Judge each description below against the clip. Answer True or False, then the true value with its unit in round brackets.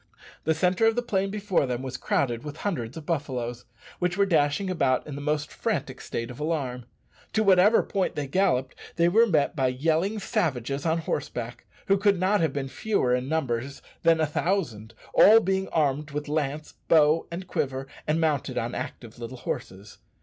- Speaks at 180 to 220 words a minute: True (185 wpm)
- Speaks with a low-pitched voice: False (150 Hz)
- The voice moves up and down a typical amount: False (5.9 semitones)